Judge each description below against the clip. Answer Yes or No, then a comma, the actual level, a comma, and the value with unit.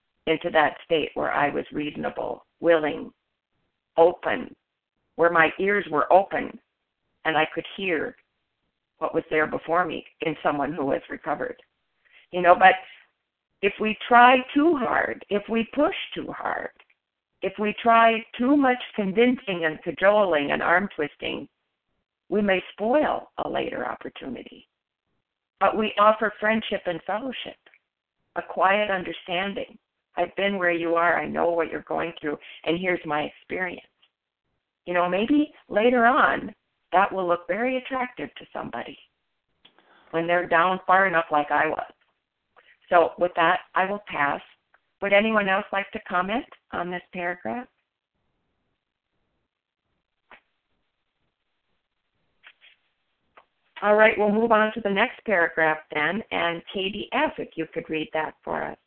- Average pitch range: Yes, average, 4.7 semitones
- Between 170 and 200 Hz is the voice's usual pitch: Yes, high, 190 Hz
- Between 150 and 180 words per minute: No, average, 140 wpm